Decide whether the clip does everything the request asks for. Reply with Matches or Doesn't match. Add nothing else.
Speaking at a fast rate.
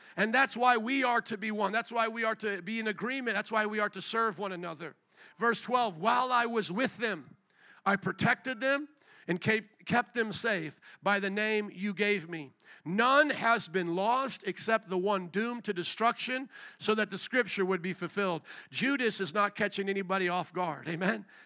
Doesn't match